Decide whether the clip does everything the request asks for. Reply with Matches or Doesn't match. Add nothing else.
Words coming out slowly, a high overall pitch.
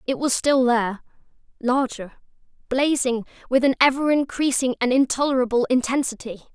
Matches